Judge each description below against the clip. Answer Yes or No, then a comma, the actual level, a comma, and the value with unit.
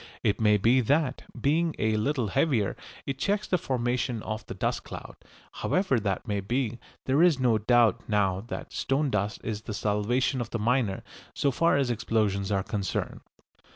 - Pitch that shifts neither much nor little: Yes, average, 4.3 semitones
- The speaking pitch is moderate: No, low, 120 Hz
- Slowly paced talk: No, average, 175 wpm